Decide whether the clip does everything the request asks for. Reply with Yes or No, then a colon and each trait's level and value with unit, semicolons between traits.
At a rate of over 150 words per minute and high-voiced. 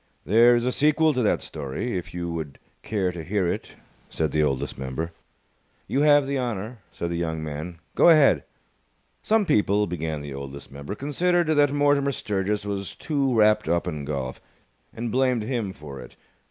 No: average, 180 wpm; low, 100 Hz